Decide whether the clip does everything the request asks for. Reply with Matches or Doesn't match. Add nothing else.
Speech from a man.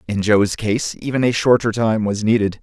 Matches